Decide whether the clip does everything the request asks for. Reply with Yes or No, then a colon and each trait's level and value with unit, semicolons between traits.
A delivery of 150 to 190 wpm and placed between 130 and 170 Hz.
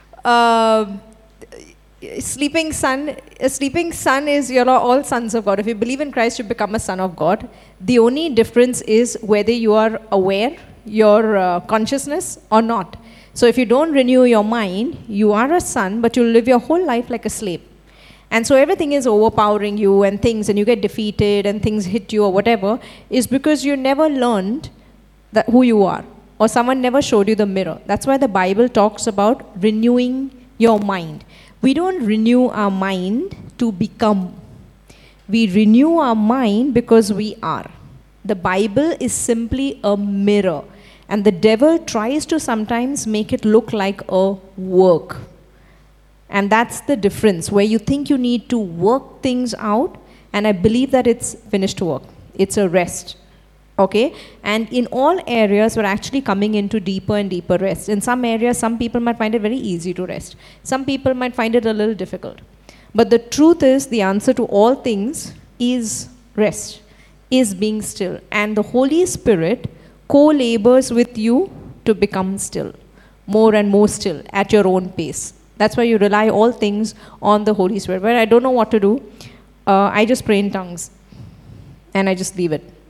No: average, 180 wpm; high, 220 Hz